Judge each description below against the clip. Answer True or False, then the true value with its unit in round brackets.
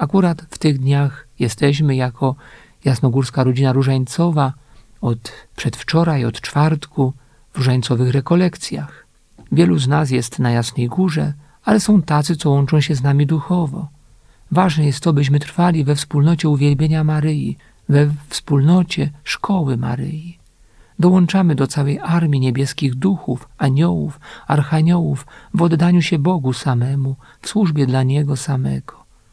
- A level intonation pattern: False (3.6 semitones)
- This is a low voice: False (145 Hz)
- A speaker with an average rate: True (130 wpm)